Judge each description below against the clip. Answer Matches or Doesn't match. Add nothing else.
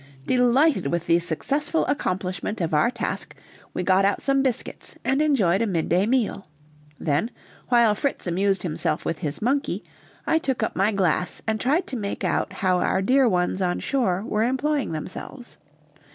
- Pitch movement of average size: Doesn't match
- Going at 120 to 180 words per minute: Matches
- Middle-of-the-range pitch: Doesn't match